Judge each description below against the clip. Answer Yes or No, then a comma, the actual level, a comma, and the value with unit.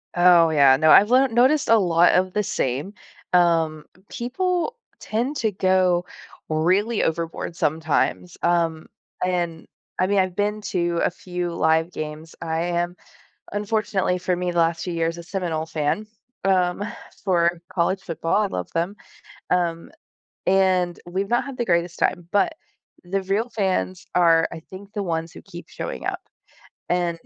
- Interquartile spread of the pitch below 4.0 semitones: Yes, average, 2.9 semitones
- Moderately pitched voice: Yes, medium, 180 Hz